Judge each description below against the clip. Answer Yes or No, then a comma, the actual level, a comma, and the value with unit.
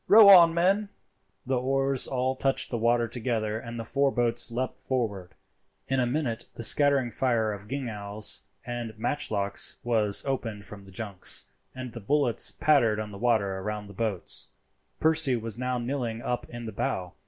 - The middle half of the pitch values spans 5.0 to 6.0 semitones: No, average, 3.7 semitones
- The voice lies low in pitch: Yes, low, 120 Hz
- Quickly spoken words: No, average, 170 wpm